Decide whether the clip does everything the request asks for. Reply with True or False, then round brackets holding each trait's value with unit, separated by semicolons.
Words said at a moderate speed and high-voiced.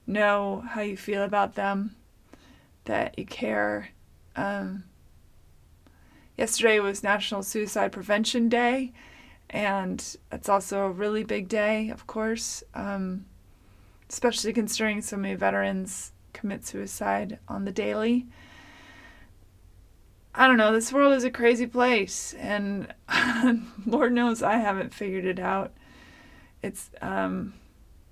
False (115 wpm; 205 Hz)